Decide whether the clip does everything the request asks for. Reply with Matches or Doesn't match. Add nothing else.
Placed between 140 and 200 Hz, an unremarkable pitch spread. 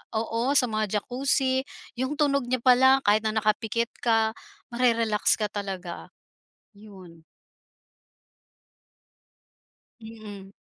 Doesn't match